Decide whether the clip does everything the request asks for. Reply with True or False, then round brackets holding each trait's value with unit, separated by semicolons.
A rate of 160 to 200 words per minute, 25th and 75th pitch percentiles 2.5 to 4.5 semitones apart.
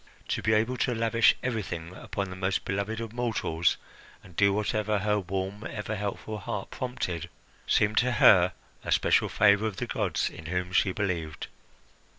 True (165 wpm; 3.0 semitones)